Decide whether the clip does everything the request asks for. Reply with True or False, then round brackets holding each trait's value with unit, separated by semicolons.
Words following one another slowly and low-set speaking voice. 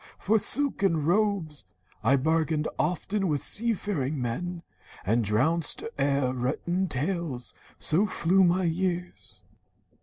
False (115 wpm; 165 Hz)